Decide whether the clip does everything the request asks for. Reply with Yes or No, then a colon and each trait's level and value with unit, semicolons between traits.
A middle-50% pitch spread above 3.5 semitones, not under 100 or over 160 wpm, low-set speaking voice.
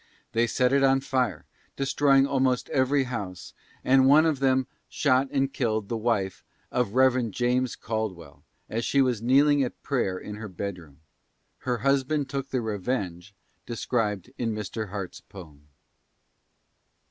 Yes: average, 4.5 semitones; average, 145 wpm; low, 125 Hz